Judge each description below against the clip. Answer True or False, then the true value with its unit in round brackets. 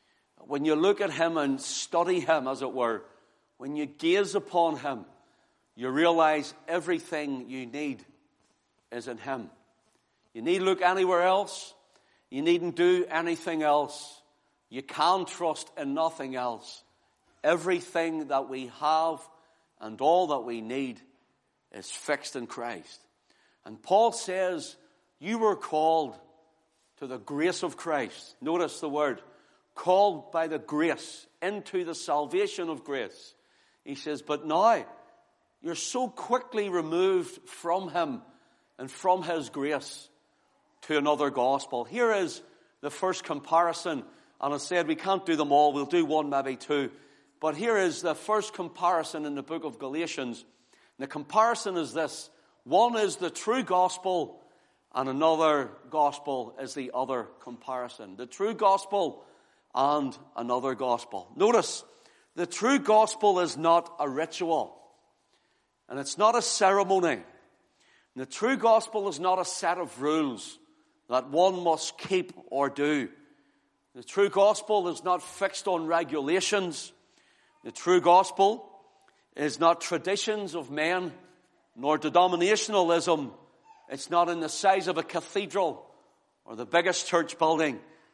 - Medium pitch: True (165 Hz)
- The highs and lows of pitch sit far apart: False (4.7 semitones)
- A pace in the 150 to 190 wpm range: False (140 wpm)